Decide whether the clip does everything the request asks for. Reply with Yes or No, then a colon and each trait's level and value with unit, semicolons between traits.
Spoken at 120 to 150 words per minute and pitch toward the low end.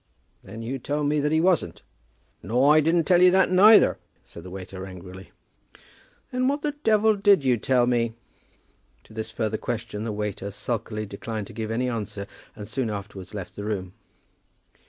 No: average, 175 wpm; low, 115 Hz